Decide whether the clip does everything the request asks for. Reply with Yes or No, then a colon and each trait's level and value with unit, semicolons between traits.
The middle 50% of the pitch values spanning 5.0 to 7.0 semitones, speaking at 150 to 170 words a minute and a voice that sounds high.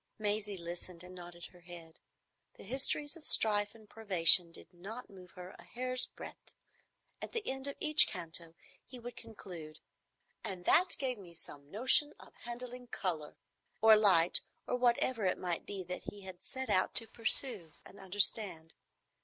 Yes: wide, 5.4 semitones; average, 165 wpm; high, 200 Hz